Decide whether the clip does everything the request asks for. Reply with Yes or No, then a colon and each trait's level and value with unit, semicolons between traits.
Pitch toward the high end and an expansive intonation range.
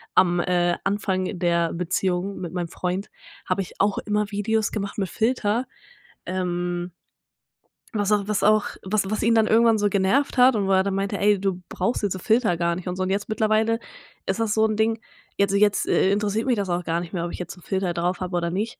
No: high, 195 Hz; average, 3.0 semitones